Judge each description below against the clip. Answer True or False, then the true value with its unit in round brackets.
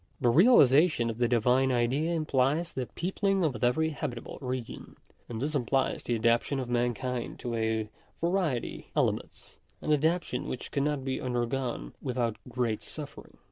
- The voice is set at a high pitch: False (130 Hz)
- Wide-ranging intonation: False (4.0 semitones)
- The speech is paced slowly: False (160 wpm)